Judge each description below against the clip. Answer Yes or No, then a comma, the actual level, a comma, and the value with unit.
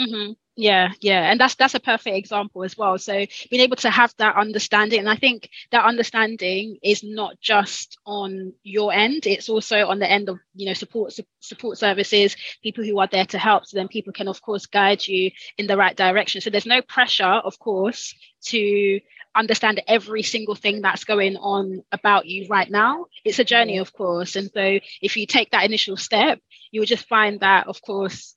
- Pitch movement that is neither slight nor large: No, narrow, 2.2 semitones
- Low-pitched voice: No, high, 205 Hz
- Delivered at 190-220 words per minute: Yes, fast, 205 wpm